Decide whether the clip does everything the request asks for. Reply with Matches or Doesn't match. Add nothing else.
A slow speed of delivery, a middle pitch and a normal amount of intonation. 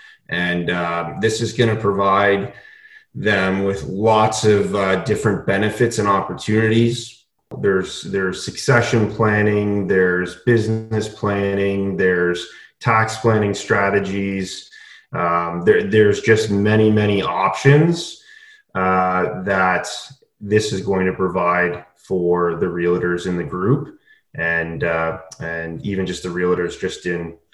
Doesn't match